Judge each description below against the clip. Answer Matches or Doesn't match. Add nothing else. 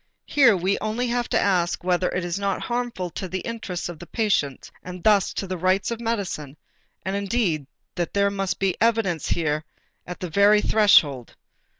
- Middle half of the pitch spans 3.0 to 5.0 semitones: Matches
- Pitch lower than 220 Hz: Matches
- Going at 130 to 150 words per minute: Doesn't match